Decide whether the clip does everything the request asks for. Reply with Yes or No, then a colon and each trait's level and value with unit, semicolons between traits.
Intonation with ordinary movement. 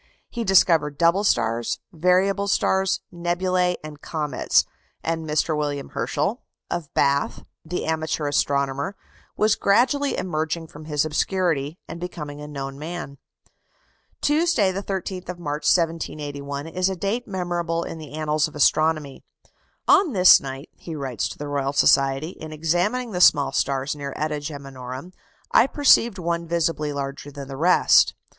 Yes: average, 4.1 semitones